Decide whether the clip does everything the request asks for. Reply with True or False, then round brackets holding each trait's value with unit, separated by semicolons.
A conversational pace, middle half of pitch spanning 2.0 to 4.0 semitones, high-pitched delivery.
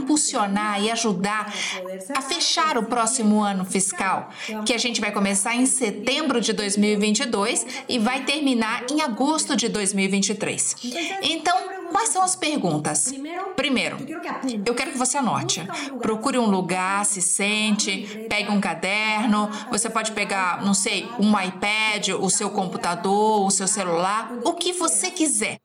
False (145 wpm; 4.8 semitones; 220 Hz)